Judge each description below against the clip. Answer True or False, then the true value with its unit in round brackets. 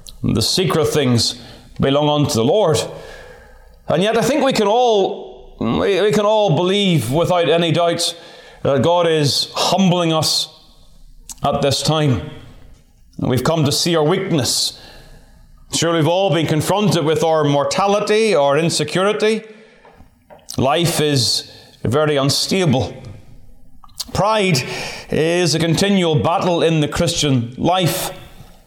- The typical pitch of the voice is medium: True (160 Hz)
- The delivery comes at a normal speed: False (125 wpm)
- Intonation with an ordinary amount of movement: True (4.6 semitones)